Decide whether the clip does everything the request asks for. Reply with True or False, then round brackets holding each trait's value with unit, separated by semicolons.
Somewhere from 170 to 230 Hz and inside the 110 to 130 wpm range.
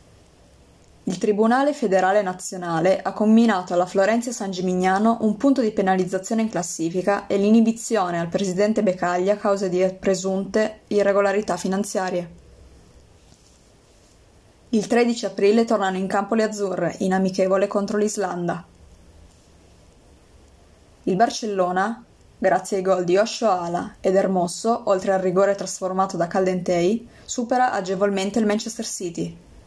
True (190 Hz; 120 wpm)